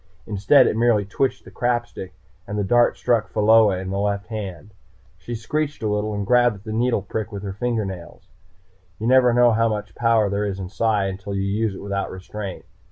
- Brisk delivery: Yes, fast, 210 wpm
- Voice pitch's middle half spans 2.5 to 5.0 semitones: Yes, average, 2.9 semitones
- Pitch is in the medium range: No, low, 105 Hz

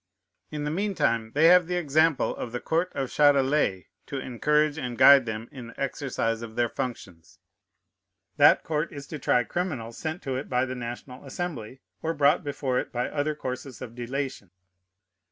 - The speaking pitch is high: No, low, 135 Hz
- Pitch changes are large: No, average, 3.9 semitones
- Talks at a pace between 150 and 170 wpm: No, average, 180 wpm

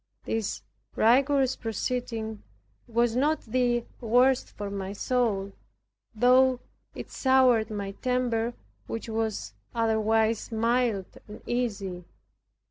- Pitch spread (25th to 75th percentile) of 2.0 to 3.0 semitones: Yes, narrow, 2.5 semitones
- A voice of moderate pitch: No, high, 230 Hz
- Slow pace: Yes, slow, 100 wpm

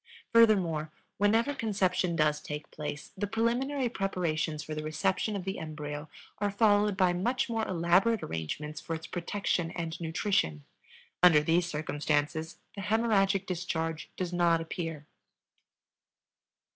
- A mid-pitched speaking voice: Yes, medium, 175 Hz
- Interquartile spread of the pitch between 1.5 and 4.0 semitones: No, average, 4.7 semitones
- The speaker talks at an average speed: No, slow, 130 wpm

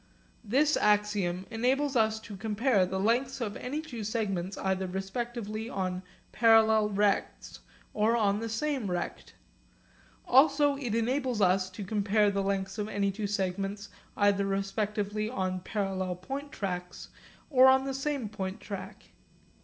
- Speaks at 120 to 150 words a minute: Yes, average, 140 wpm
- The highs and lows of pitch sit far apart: No, average, 3.4 semitones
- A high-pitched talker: Yes, high, 210 Hz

